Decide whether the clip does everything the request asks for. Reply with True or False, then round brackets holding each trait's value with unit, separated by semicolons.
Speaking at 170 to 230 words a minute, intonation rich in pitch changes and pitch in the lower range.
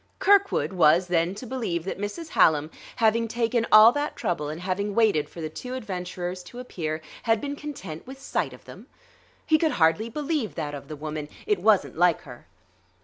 False (190 wpm; 6.7 semitones; 200 Hz)